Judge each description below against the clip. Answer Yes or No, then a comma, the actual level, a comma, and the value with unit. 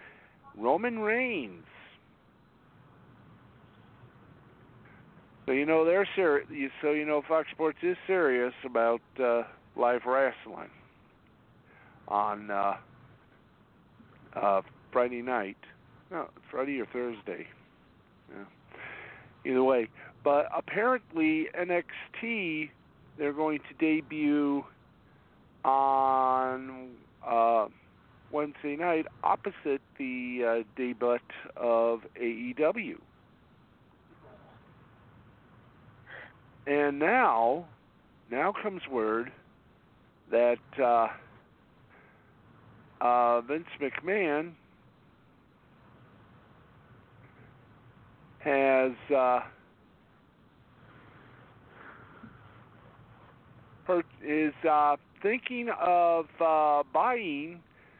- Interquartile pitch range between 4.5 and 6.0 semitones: Yes, average, 4.8 semitones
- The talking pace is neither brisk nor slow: No, slow, 70 wpm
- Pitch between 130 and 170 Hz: Yes, low, 135 Hz